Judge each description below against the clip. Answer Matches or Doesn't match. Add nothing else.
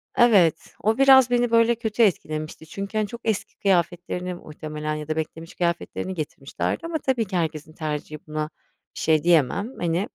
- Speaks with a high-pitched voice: Doesn't match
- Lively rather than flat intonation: Matches